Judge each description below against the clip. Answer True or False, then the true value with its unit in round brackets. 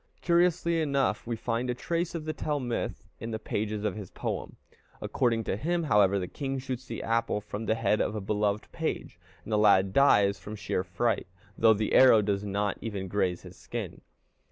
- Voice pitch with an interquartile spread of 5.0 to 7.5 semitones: False (4.3 semitones)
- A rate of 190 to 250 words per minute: True (200 wpm)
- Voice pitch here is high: False (110 Hz)